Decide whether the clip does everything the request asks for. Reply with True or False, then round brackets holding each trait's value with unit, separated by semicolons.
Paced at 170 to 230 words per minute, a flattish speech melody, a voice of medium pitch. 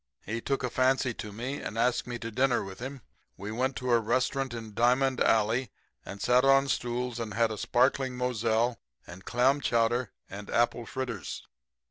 False (180 wpm; 2.2 semitones; 120 Hz)